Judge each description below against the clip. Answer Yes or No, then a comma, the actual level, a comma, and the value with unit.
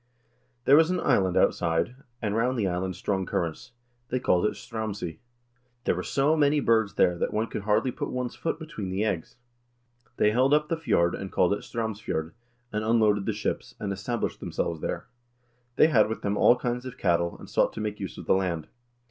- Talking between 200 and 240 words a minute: Yes, fast, 205 wpm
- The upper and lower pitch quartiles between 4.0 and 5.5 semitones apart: Yes, average, 4.7 semitones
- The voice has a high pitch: No, low, 105 Hz